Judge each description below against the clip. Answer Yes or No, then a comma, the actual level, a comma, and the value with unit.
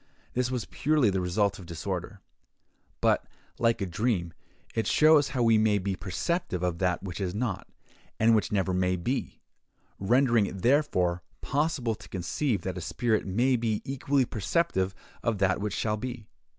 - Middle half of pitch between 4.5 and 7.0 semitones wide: Yes, average, 5.0 semitones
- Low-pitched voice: Yes, low, 105 Hz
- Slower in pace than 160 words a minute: No, average, 165 wpm